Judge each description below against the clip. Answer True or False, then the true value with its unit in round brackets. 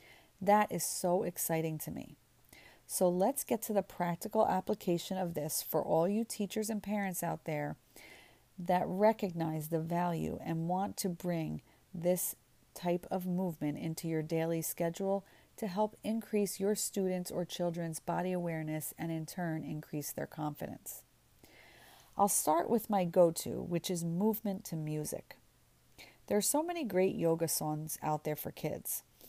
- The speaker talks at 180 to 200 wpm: False (155 wpm)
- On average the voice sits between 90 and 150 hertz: False (175 Hz)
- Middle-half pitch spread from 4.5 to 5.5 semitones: False (3.5 semitones)